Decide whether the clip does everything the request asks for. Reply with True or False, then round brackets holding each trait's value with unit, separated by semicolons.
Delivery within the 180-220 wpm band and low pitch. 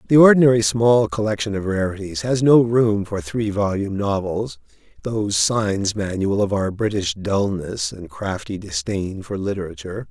False (150 wpm; 100 Hz)